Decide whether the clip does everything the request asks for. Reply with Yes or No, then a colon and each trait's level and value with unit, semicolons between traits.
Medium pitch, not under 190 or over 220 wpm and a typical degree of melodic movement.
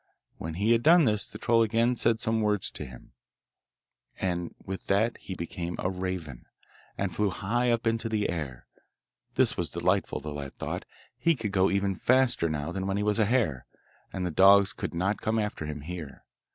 No: low, 100 Hz; average, 195 wpm; average, 4.5 semitones